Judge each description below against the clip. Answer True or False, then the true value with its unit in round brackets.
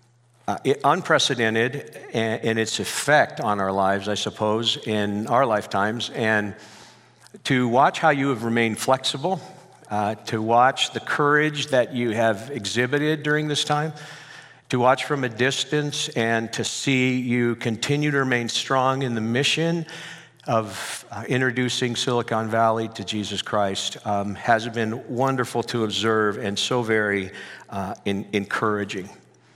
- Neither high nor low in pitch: False (120 Hz)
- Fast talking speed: False (145 wpm)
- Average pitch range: True (3.9 semitones)